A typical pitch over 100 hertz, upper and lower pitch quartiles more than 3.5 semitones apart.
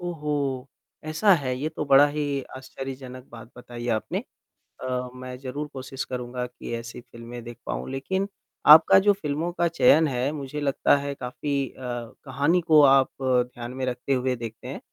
No: low, 135 Hz; average, 2.9 semitones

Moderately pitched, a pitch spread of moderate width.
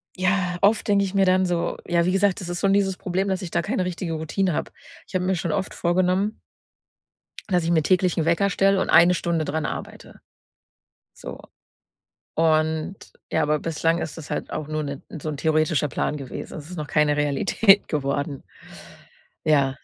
Yes: medium, 170 Hz; average, 3.3 semitones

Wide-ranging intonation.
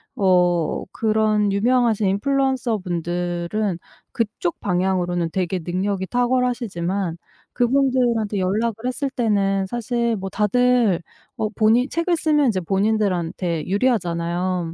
No: average, 4.9 semitones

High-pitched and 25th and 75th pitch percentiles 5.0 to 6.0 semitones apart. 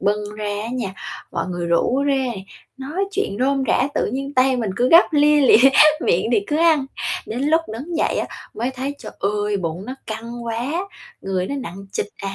Yes: very high, 250 Hz; average, 5.3 semitones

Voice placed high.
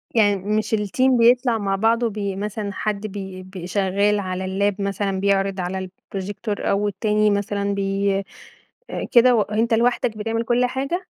Yes: high, 205 Hz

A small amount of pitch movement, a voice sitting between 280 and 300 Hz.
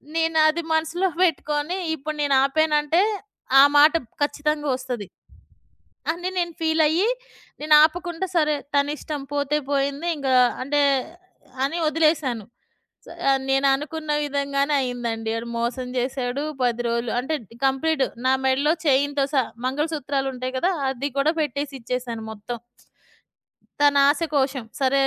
No: average, 3.0 semitones; very high, 285 Hz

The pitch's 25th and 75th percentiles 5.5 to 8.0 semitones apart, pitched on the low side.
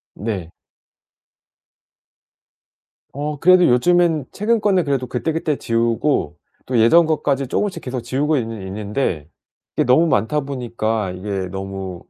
Yes: wide, 6.4 semitones; low, 125 Hz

